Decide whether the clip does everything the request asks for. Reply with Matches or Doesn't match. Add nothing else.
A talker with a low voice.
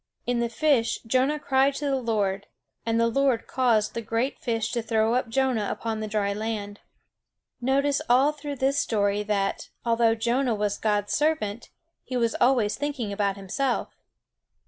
Doesn't match